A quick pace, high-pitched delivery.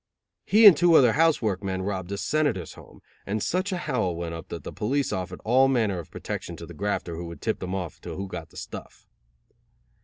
No: fast, 225 wpm; low, 100 Hz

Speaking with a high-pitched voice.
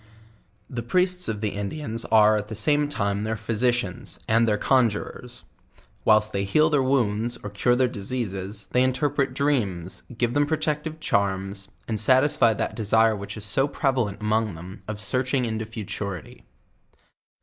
No: low, 110 Hz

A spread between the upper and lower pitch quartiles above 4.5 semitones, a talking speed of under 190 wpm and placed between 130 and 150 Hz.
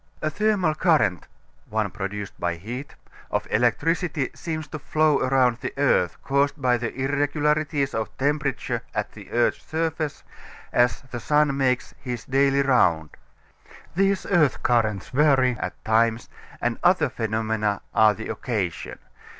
Yes: average, 5.2 semitones; slow, 135 wpm; low, 135 Hz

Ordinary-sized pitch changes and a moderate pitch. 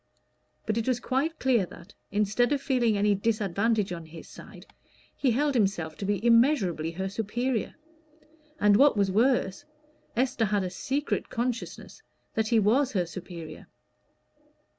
No: average, 4.3 semitones; high, 215 Hz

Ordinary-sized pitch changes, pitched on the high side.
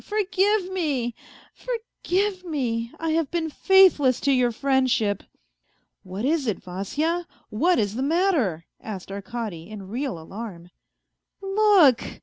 No: wide, 8.9 semitones; very high, 270 Hz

